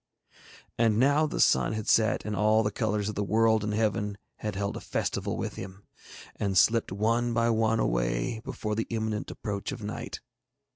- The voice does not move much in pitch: Yes, narrow, 1.7 semitones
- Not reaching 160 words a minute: No, average, 185 wpm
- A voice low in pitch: Yes, low, 110 Hz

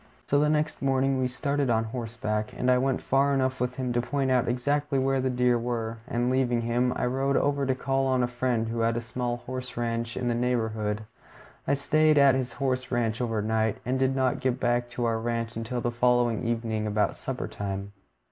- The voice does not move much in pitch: Yes, narrow, 2.2 semitones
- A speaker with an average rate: No, fast, 210 wpm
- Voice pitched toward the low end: Yes, low, 125 Hz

